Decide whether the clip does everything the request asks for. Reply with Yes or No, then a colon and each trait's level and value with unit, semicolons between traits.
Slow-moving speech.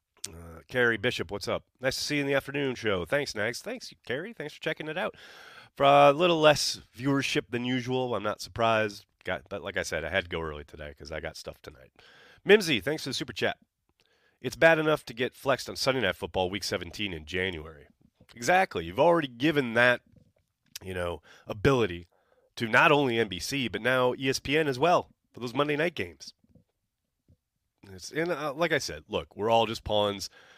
No: average, 195 wpm